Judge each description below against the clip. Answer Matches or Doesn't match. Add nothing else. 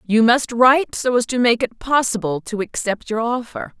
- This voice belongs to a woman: Matches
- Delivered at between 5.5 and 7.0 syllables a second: Doesn't match